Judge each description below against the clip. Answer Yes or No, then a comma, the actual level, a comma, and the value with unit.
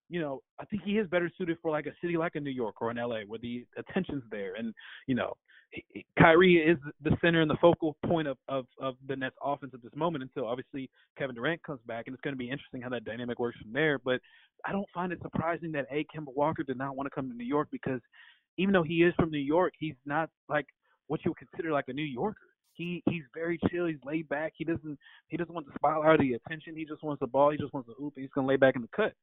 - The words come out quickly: Yes, fast, 275 wpm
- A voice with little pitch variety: No, average, 3.7 semitones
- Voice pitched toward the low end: No, medium, 150 Hz